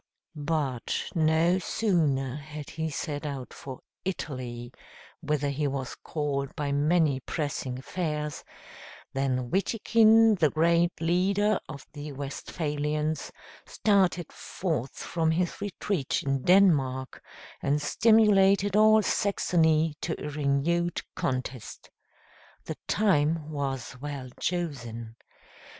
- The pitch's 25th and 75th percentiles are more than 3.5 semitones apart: Yes, average, 4.2 semitones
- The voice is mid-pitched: Yes, medium, 150 Hz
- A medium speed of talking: No, slow, 105 wpm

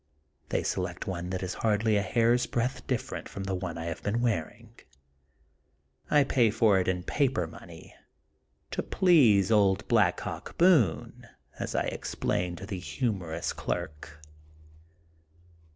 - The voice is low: Yes, low, 100 Hz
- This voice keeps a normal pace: Yes, average, 150 wpm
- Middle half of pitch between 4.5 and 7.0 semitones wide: Yes, average, 4.9 semitones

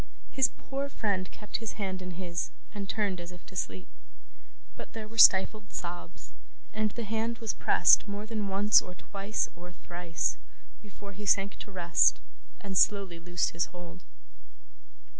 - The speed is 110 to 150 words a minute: No, average, 160 wpm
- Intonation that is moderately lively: Yes, average, 3.1 semitones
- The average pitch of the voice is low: No, high, 195 Hz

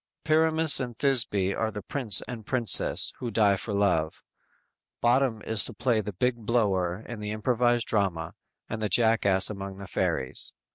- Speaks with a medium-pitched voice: No, low, 110 Hz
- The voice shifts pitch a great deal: No, average, 3.5 semitones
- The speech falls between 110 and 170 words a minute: Yes, average, 160 wpm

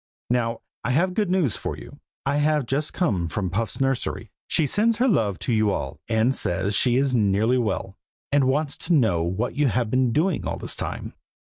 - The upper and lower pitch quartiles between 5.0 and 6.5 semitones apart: Yes, wide, 5.5 semitones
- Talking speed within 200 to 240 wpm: Yes, fast, 205 wpm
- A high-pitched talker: No, low, 125 Hz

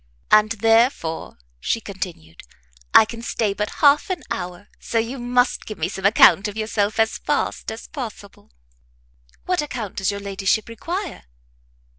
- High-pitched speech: Yes, high, 220 Hz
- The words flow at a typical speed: Yes, average, 150 wpm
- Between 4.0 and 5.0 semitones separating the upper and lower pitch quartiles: No, average, 3.3 semitones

